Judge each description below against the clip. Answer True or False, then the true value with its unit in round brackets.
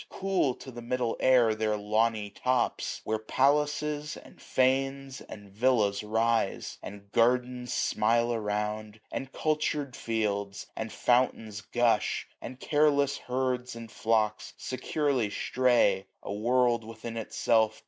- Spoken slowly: True (125 wpm)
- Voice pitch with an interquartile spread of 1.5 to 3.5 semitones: True (3.1 semitones)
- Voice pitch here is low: True (115 Hz)